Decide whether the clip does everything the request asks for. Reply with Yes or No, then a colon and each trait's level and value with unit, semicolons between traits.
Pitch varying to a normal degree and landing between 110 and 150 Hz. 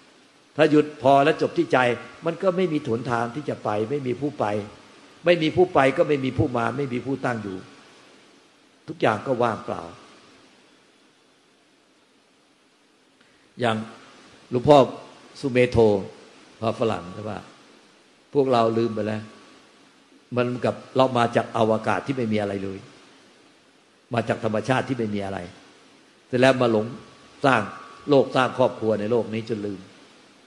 Yes: average, 3.8 semitones; low, 120 Hz